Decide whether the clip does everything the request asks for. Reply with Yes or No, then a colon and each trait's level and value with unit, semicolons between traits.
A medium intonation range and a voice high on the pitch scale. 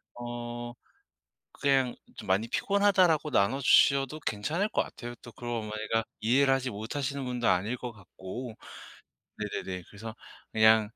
No: average, 3.9 semitones; low, 120 Hz